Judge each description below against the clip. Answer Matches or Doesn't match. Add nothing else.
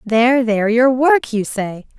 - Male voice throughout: Doesn't match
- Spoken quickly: Doesn't match